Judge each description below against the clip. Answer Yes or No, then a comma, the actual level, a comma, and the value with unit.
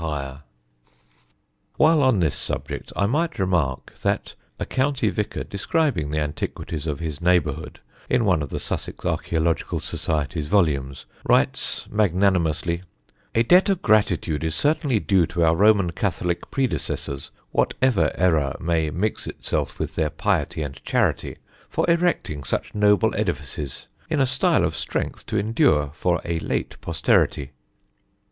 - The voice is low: Yes, very low, 85 Hz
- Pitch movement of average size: No, wide, 6.0 semitones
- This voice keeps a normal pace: Yes, average, 145 wpm